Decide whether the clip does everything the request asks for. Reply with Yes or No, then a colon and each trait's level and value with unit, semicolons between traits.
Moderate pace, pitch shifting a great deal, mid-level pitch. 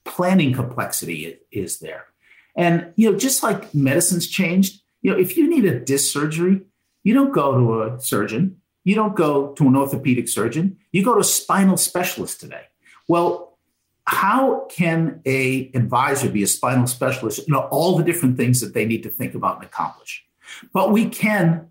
Yes: average, 180 wpm; wide, 6.6 semitones; medium, 170 Hz